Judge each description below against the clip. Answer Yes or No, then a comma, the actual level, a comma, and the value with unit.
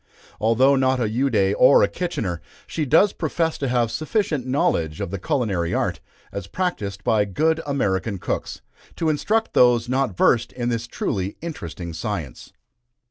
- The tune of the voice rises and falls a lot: Yes, wide, 6.8 semitones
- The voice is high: No, low, 120 Hz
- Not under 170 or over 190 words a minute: No, average, 155 wpm